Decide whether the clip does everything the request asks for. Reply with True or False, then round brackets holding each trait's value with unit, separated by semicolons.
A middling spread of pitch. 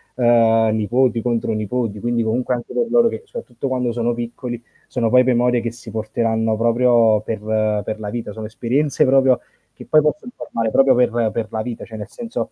False (2.2 semitones)